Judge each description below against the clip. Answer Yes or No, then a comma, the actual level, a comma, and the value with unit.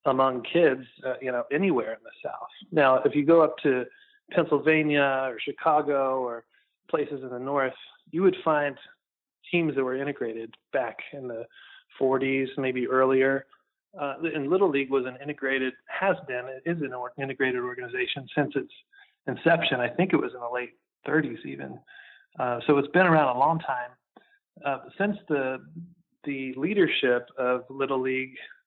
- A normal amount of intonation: Yes, average, 4.3 semitones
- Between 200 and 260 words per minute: No, average, 165 wpm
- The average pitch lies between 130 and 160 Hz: Yes, medium, 140 Hz